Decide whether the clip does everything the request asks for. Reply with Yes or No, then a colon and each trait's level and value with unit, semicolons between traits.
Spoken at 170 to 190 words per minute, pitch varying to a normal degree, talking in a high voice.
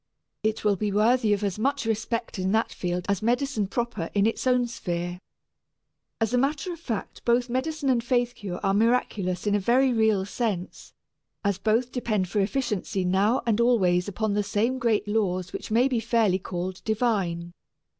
Yes: average, 180 wpm; average, 3.8 semitones; high, 220 Hz